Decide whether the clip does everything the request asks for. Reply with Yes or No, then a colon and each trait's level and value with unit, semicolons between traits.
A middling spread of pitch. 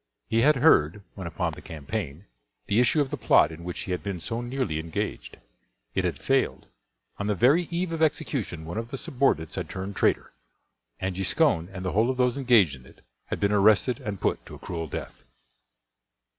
No: wide, 6.7 semitones